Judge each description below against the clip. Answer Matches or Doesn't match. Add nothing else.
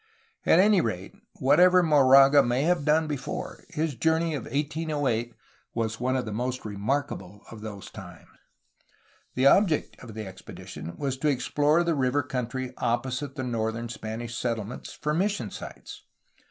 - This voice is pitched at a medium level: Doesn't match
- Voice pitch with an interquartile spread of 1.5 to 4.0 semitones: Doesn't match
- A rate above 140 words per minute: Matches